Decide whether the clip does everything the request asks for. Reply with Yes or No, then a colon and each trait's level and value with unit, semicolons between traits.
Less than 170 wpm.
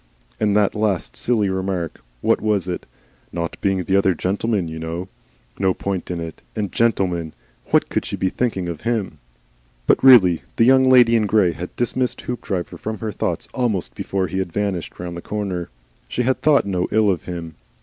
No: average, 190 wpm